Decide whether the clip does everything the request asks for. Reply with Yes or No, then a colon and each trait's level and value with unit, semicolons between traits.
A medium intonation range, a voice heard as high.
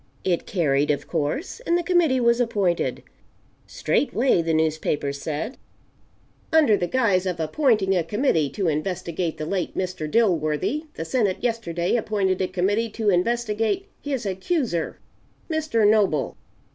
No: wide, 6.0 semitones; high, 195 Hz